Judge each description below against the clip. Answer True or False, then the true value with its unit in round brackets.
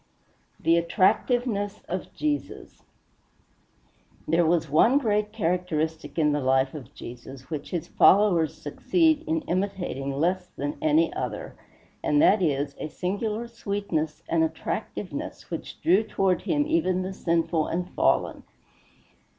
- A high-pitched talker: False (175 Hz)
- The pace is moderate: False (130 wpm)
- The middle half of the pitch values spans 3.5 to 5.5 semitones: True (5.1 semitones)